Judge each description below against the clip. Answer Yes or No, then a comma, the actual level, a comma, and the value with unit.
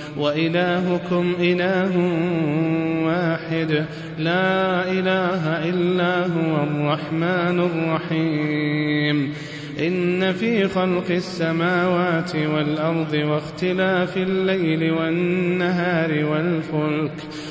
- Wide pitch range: No, narrow, 2.6 semitones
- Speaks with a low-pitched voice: No, medium, 165 Hz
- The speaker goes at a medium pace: No, slow, 60 wpm